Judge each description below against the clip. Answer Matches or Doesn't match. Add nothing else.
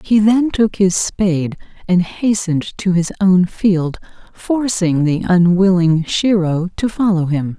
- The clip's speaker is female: Matches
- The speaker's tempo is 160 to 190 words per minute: Doesn't match